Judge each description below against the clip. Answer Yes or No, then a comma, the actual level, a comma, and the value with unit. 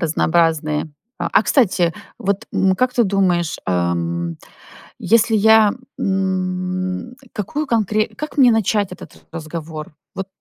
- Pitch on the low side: No, medium, 185 Hz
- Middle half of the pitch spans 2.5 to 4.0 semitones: No, average, 4.8 semitones